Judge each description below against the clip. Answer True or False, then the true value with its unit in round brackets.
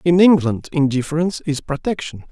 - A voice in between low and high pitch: True (155 Hz)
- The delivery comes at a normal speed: False (130 wpm)